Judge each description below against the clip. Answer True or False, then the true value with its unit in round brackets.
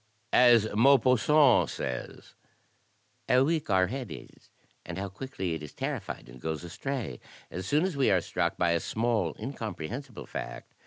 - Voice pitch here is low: True (110 Hz)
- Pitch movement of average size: False (7.4 semitones)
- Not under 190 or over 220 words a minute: False (155 wpm)